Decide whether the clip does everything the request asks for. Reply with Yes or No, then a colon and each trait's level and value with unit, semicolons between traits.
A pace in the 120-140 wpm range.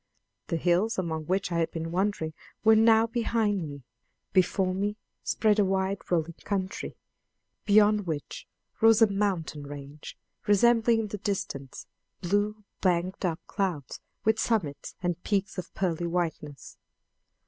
Yes: slow, 135 wpm